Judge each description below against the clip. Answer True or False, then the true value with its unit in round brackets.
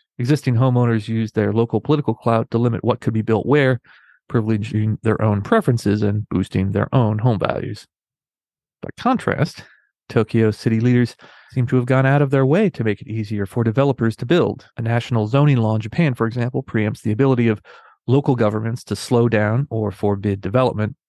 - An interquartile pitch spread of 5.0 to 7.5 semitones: False (3.2 semitones)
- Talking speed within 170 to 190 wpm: True (185 wpm)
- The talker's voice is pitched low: True (115 Hz)